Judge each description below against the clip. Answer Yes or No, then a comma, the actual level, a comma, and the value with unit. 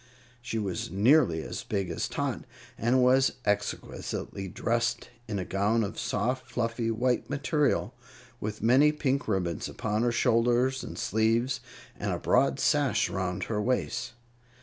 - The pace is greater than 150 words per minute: No, average, 145 wpm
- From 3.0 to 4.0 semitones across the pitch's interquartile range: Yes, average, 3.7 semitones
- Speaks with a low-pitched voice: Yes, low, 115 Hz